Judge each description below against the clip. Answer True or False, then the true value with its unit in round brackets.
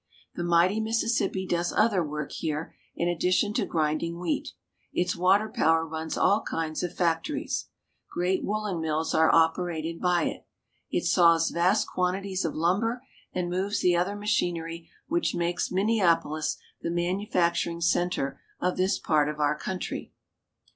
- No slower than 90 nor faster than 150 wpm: True (145 wpm)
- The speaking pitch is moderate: True (175 Hz)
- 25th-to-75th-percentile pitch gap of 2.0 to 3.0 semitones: True (2.7 semitones)